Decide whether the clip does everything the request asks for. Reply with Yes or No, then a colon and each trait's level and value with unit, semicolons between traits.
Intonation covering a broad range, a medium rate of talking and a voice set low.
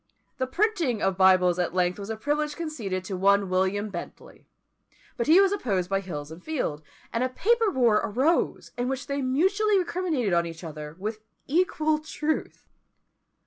No: wide, 8.8 semitones; average, 170 wpm; high, 230 Hz